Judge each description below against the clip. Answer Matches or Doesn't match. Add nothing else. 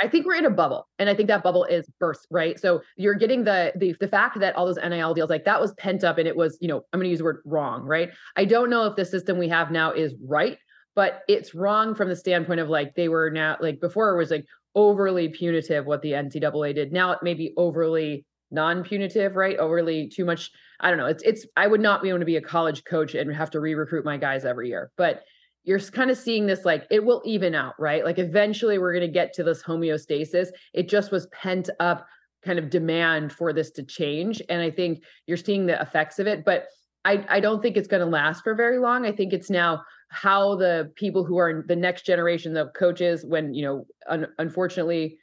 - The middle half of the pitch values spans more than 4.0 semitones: Doesn't match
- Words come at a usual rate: Doesn't match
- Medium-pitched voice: Matches